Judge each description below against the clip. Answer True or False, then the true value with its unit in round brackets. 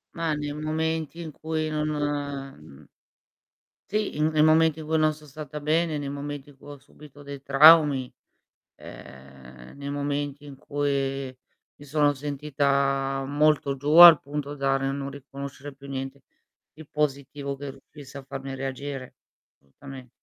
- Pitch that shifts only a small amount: True (1.8 semitones)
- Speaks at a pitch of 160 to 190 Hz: False (145 Hz)